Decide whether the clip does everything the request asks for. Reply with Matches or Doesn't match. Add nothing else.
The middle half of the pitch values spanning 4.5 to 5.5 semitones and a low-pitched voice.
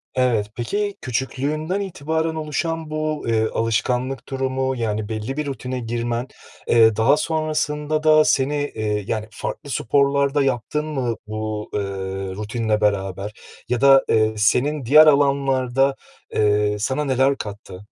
Matches